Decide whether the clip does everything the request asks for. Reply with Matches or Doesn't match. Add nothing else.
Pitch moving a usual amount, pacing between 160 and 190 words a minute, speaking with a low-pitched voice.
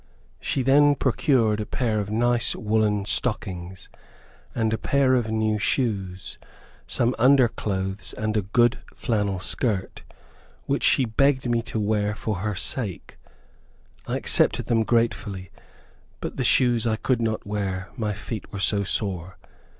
Doesn't match